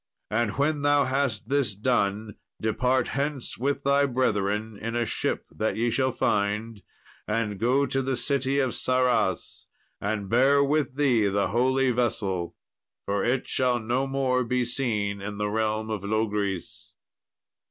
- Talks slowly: No, average, 150 wpm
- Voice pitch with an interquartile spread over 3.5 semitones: Yes, average, 4.0 semitones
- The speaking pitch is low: Yes, low, 120 Hz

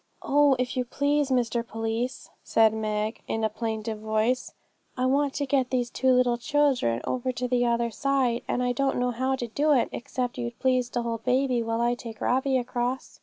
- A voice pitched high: Yes, high, 245 Hz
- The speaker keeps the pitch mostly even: Yes, narrow, 2.1 semitones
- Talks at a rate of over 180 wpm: Yes, average, 200 wpm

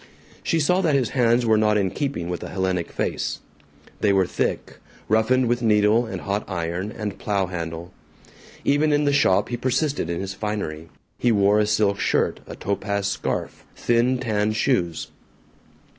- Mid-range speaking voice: No, low, 105 Hz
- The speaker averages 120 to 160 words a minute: No, average, 170 wpm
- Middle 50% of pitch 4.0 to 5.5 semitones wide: Yes, average, 4.3 semitones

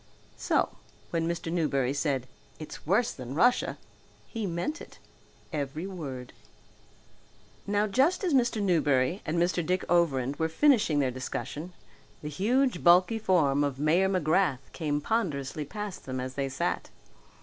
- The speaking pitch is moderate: Yes, medium, 165 Hz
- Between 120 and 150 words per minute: Yes, average, 140 wpm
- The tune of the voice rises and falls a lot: Yes, wide, 5.7 semitones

